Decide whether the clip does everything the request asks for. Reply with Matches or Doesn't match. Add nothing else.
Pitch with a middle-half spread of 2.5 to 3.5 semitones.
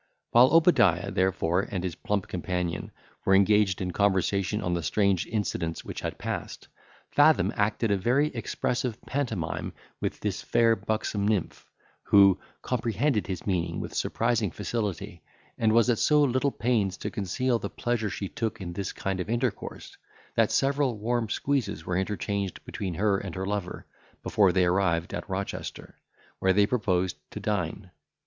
Doesn't match